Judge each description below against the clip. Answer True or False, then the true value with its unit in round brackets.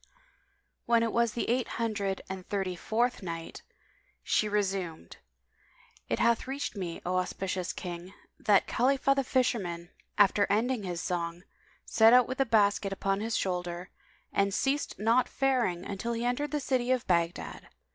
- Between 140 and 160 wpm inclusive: True (155 wpm)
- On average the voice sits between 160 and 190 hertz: False (210 Hz)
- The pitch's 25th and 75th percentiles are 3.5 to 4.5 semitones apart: False (4.9 semitones)